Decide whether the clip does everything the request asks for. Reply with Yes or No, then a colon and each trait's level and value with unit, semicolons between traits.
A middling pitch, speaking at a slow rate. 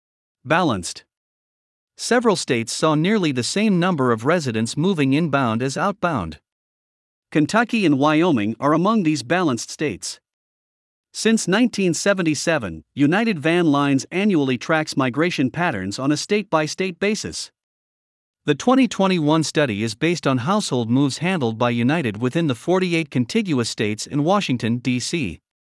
Yes: medium, 155 Hz; slow, 130 wpm